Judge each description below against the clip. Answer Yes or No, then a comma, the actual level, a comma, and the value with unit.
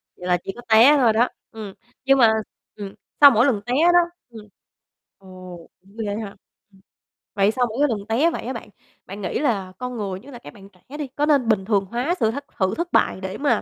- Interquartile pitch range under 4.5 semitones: No, average, 5.0 semitones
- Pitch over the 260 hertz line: No, high, 225 Hz